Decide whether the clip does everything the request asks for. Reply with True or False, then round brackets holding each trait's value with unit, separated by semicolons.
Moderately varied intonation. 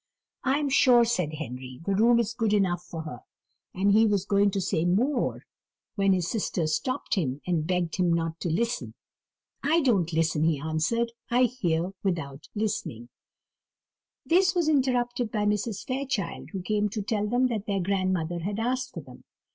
False (5.8 semitones)